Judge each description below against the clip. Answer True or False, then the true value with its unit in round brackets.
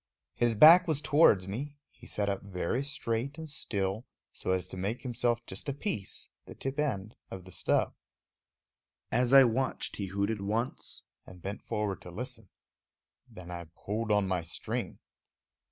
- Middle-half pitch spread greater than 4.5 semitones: True (5.6 semitones)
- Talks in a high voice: False (110 Hz)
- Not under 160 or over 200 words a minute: True (165 wpm)